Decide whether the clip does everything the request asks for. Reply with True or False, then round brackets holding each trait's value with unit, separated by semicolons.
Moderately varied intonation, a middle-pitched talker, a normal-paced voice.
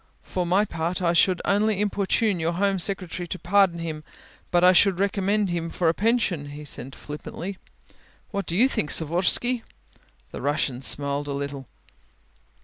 True (3.8 semitones; 175 Hz; 165 wpm)